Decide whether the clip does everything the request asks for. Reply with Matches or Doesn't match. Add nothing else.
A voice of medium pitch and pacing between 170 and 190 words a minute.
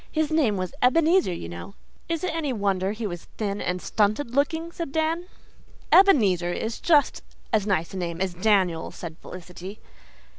Doesn't match